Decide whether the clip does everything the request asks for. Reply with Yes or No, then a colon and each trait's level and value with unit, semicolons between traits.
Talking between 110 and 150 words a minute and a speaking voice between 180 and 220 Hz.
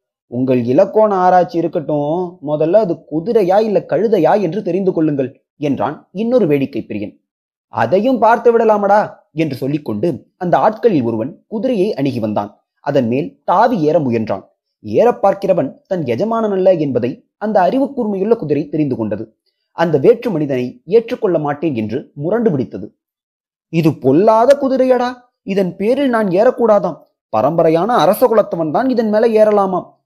Yes: fast, 130 wpm; high, 190 Hz